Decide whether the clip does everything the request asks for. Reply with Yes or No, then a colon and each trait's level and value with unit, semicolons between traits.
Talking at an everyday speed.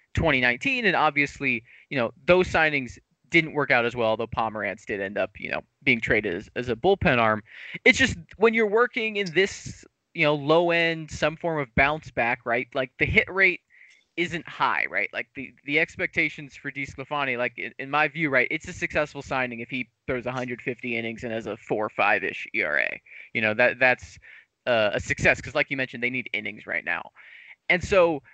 Yes: average, 195 wpm